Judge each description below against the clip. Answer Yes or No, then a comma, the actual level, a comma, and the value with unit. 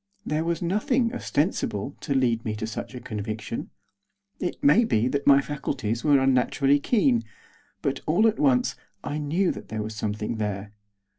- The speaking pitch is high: No, low, 135 Hz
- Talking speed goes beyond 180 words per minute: No, average, 165 wpm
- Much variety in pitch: Yes, wide, 6.2 semitones